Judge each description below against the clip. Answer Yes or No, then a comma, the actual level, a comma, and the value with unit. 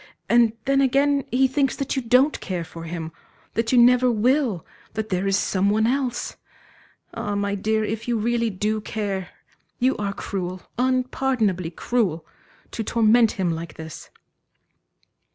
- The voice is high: Yes, high, 220 Hz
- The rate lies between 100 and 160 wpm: Yes, average, 150 wpm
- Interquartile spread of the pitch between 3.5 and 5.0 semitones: Yes, average, 4.5 semitones